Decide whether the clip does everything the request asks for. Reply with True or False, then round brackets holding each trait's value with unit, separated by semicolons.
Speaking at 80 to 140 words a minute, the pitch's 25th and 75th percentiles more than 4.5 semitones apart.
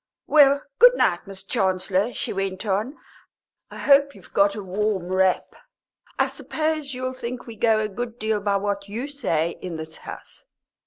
False (170 wpm; 5.1 semitones)